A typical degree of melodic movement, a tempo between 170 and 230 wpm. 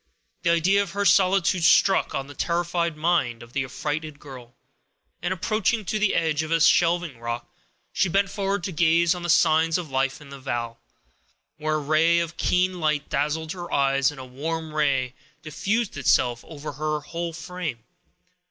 Yes: average, 3.7 semitones; average, 180 wpm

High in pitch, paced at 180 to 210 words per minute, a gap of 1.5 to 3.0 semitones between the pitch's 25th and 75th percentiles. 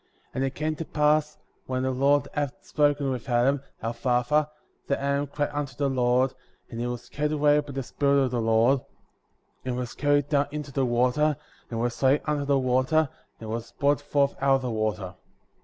No: low, 135 Hz; average, 200 wpm; average, 2.7 semitones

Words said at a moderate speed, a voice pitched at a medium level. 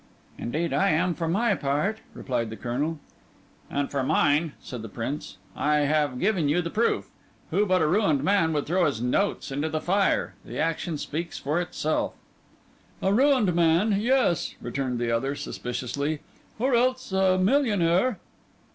Yes: average, 155 wpm; medium, 165 Hz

